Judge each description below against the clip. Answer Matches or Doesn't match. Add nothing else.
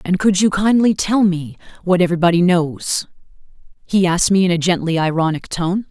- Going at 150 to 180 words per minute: Matches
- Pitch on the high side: Doesn't match